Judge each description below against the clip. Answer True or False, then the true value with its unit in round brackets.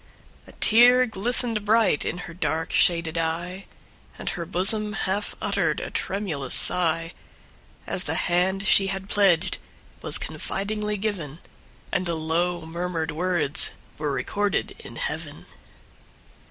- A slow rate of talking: True (115 wpm)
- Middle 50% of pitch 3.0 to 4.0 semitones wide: True (3.7 semitones)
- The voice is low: False (180 Hz)